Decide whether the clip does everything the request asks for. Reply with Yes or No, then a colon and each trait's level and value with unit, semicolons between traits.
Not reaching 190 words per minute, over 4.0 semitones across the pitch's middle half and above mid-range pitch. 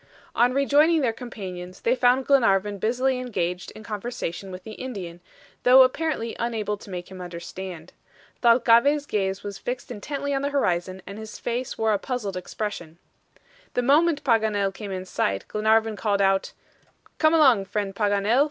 Yes: average, 160 wpm; average, 4.7 semitones; high, 220 Hz